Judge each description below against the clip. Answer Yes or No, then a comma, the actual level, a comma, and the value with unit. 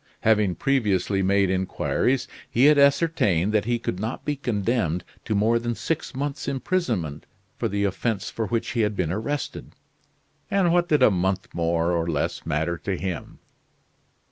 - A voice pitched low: Yes, low, 105 Hz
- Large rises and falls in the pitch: Yes, wide, 6.1 semitones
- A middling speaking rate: Yes, average, 165 wpm